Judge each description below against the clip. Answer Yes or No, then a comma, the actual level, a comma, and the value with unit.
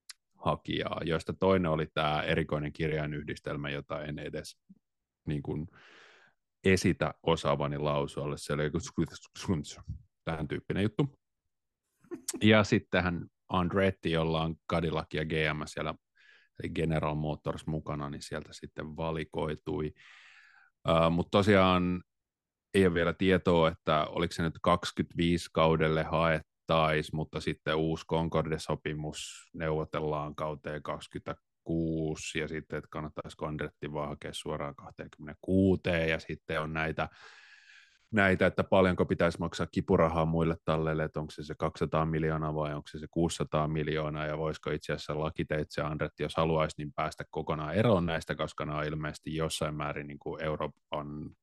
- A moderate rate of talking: Yes, average, 135 wpm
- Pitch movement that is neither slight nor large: No, narrow, 1.9 semitones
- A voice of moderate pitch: No, very low, 80 Hz